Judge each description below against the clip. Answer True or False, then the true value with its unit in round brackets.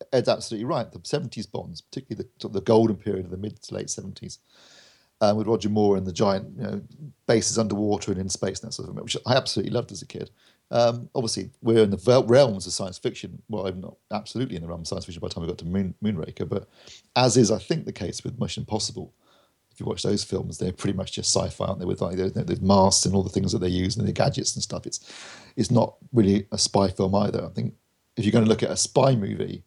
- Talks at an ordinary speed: False (265 wpm)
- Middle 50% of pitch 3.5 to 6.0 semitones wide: False (2.9 semitones)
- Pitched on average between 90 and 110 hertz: True (105 Hz)